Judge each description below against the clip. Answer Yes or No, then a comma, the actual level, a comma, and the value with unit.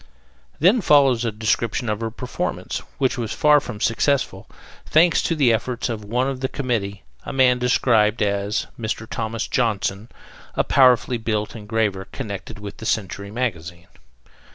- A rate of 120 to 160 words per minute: Yes, average, 155 wpm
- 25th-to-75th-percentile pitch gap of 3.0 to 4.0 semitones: Yes, average, 3.5 semitones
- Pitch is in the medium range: No, low, 115 Hz